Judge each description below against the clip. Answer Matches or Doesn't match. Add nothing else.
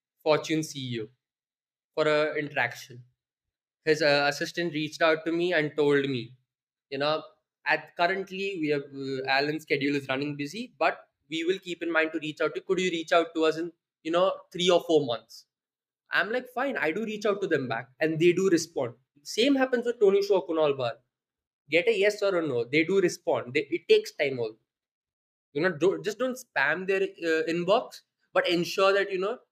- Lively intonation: Doesn't match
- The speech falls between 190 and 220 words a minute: Matches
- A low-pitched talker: Doesn't match